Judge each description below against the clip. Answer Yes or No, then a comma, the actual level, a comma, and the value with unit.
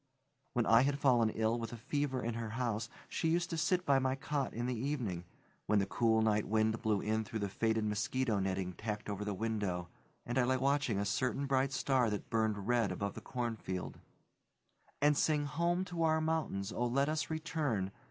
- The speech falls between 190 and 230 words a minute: Yes, average, 200 wpm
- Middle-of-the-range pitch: No, low, 120 Hz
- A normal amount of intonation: Yes, average, 4.7 semitones